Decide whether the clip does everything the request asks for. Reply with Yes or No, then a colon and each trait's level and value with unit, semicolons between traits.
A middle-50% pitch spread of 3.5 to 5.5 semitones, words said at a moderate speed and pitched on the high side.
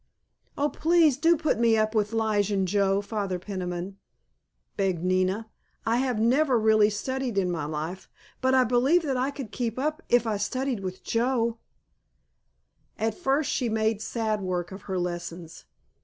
Yes: average, 4.9 semitones; average, 165 wpm; high, 220 Hz